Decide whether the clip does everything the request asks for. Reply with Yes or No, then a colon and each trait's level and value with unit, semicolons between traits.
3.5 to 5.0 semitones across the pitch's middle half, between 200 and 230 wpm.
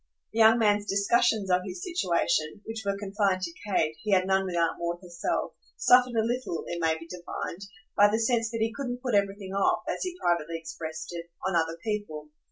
Yes: average, 4.5 semitones; fast, 205 wpm